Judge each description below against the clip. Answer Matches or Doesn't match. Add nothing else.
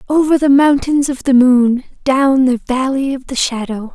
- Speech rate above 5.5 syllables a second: Doesn't match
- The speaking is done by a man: Doesn't match